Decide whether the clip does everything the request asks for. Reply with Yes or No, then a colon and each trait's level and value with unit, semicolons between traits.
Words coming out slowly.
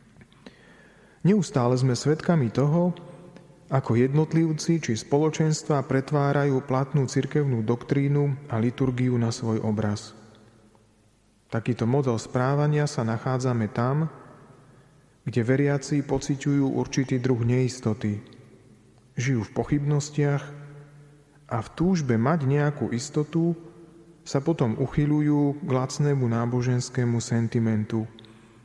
Yes: slow, 95 wpm